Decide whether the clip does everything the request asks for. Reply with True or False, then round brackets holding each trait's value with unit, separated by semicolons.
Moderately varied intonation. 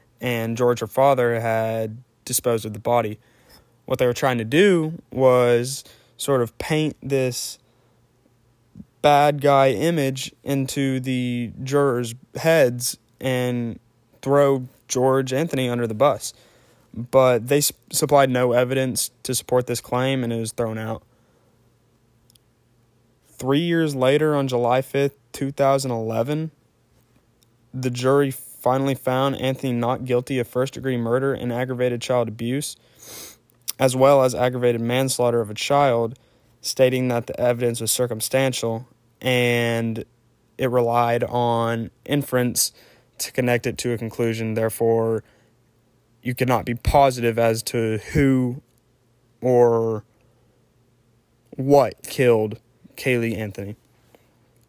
False (2.0 semitones)